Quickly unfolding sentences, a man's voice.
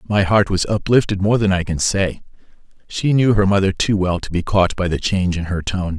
Yes: fast, 230 wpm; male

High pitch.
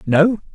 No: medium, 180 Hz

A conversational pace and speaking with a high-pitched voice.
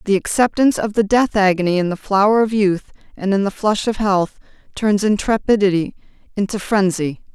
Yes: average, 170 wpm; high, 200 Hz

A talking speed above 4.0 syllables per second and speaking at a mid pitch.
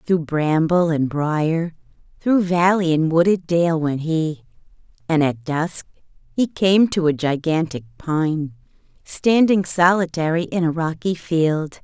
No: 3.8 syllables/s; medium, 165 Hz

